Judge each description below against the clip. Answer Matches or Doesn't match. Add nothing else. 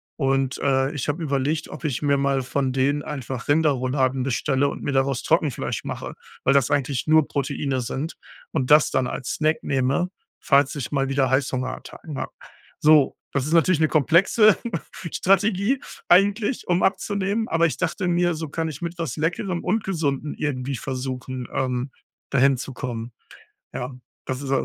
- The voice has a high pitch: Doesn't match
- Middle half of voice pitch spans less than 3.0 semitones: Doesn't match